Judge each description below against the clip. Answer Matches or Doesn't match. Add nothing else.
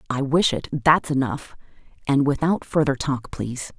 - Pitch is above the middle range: Doesn't match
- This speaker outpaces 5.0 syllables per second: Doesn't match